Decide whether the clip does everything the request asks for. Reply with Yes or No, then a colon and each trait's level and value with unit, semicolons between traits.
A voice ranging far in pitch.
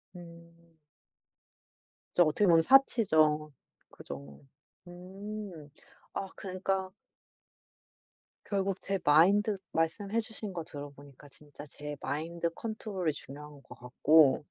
No: average, 4.7 semitones